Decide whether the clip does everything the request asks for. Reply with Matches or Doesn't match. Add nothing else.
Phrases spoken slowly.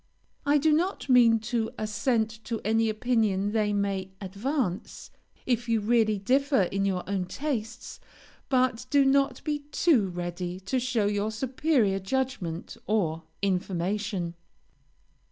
Matches